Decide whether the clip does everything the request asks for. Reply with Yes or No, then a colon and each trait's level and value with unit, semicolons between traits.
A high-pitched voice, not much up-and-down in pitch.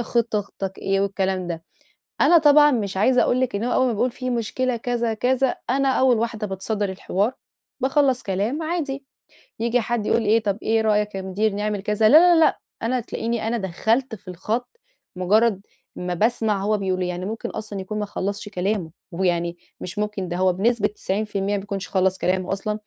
No: high, 210 Hz; average, 3.7 semitones